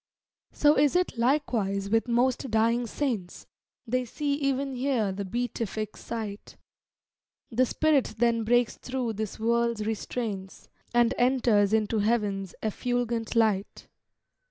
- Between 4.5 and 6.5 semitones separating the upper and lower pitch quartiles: No, average, 2.8 semitones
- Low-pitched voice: No, high, 235 Hz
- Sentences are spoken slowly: Yes, slow, 120 wpm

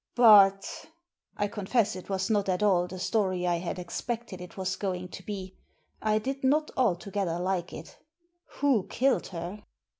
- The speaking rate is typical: Yes, average, 170 wpm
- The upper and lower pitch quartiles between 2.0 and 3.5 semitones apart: Yes, average, 3.2 semitones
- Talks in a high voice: Yes, high, 195 Hz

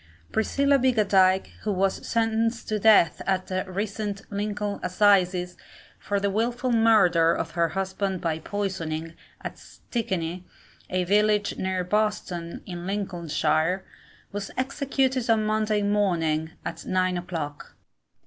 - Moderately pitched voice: No, high, 195 Hz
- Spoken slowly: Yes, slow, 120 wpm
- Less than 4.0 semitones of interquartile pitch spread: Yes, average, 3.2 semitones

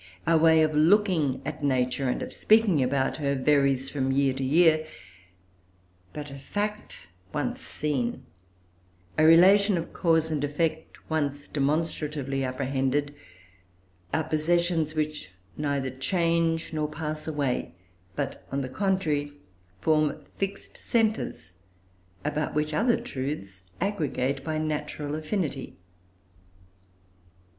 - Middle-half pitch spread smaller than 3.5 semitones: Yes, average, 2.9 semitones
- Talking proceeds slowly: Yes, slow, 115 wpm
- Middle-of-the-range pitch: Yes, medium, 150 Hz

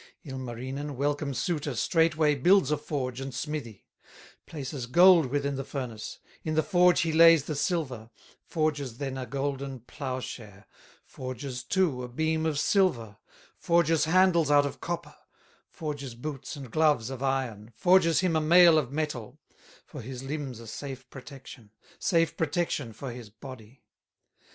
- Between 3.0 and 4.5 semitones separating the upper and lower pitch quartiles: Yes, average, 3.8 semitones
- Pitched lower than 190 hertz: Yes, medium, 140 Hz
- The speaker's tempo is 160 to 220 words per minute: No, average, 145 wpm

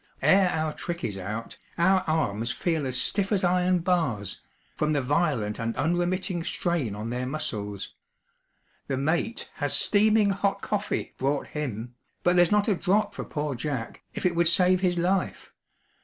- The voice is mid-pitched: Yes, medium, 165 Hz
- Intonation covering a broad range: Yes, wide, 6.5 semitones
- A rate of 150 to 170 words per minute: Yes, average, 165 wpm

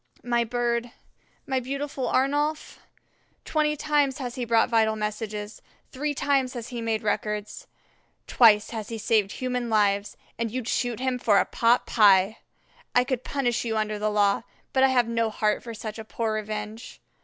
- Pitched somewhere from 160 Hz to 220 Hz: No, high, 230 Hz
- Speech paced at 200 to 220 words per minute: No, average, 170 wpm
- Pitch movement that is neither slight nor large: Yes, average, 3.1 semitones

